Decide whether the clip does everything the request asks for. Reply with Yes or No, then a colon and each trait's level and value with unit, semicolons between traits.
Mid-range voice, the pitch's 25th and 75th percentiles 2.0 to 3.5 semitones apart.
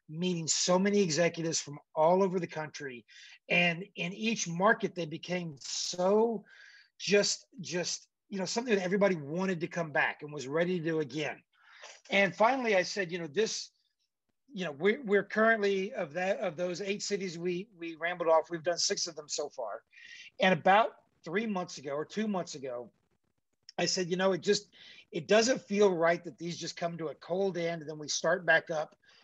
Yes: medium, 180 Hz; average, 3.2 semitones